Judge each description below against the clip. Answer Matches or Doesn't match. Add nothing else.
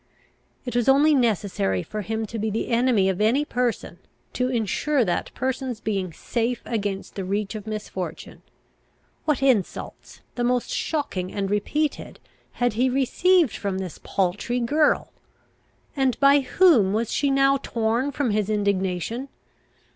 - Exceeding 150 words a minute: Doesn't match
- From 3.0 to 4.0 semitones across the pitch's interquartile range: Doesn't match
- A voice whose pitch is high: Matches